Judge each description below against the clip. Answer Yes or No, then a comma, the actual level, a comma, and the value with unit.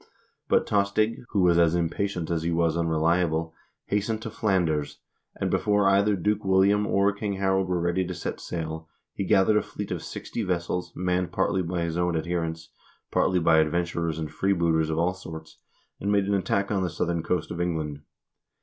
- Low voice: Yes, very low, 90 Hz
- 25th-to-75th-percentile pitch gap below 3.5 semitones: Yes, average, 3.1 semitones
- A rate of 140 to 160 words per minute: No, average, 185 wpm